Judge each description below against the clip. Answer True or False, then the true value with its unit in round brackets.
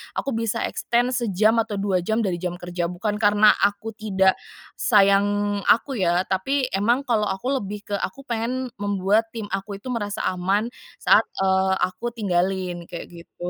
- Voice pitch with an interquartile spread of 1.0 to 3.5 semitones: True (3.0 semitones)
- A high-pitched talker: True (205 Hz)